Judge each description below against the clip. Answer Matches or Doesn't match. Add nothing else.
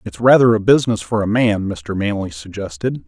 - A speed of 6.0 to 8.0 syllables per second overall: Doesn't match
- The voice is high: Doesn't match